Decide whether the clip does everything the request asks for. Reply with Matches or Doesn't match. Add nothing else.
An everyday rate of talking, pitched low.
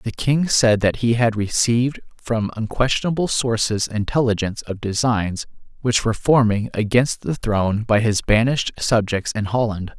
Matches